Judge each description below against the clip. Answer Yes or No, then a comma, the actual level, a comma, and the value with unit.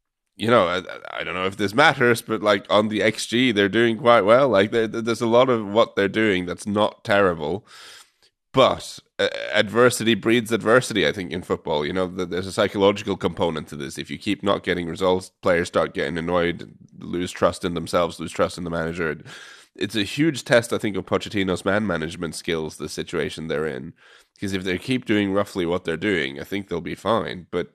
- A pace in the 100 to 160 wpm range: No, fast, 205 wpm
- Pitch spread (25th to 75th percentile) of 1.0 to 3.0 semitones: No, average, 4.1 semitones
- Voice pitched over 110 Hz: No, low, 100 Hz